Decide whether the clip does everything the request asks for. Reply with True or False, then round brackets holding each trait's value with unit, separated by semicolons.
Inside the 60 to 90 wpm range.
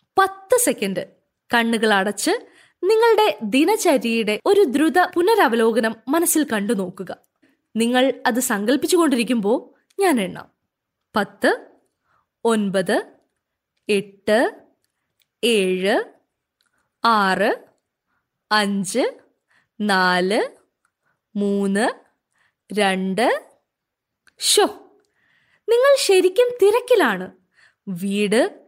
True (65 wpm)